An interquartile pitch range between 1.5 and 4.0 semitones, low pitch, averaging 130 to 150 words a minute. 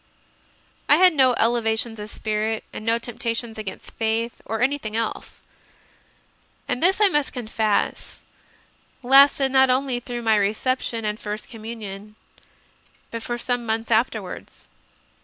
No: narrow, 2.5 semitones; high, 230 Hz; slow, 135 wpm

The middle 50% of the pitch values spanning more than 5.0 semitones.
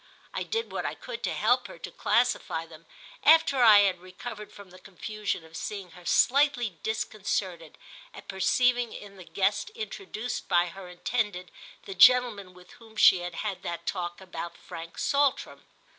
Yes: wide, 5.4 semitones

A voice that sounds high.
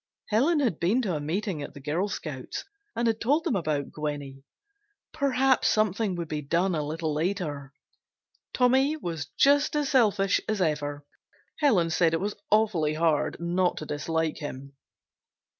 No: medium, 175 Hz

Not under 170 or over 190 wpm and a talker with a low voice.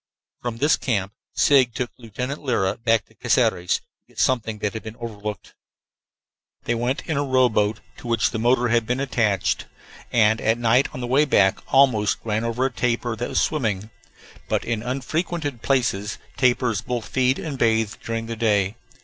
Yes: average, 175 wpm; low, 115 Hz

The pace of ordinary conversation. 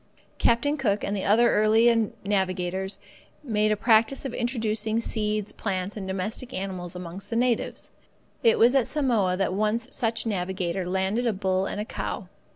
Yes: average, 165 wpm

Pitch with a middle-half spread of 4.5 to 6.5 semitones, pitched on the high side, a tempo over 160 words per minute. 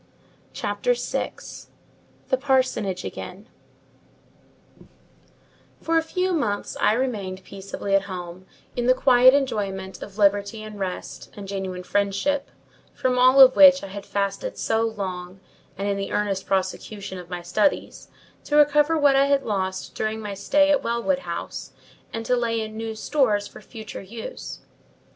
No: average, 5.2 semitones; high, 215 Hz; average, 150 wpm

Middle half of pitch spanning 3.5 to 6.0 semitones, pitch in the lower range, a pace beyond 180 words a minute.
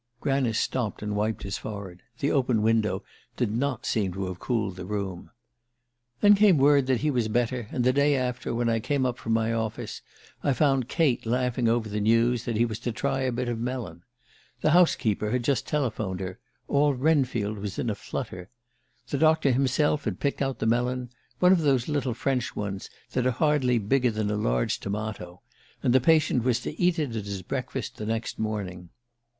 Yes: average, 4.0 semitones; low, 120 Hz; average, 200 wpm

